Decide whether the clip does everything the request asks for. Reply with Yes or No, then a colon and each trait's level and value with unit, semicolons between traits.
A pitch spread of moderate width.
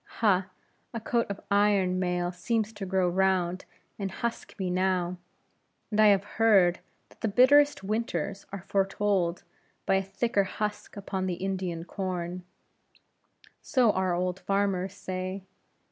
No: narrow, 2.1 semitones